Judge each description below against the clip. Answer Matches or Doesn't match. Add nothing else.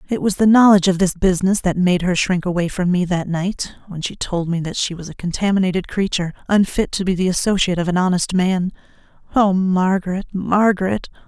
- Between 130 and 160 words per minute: Doesn't match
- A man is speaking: Doesn't match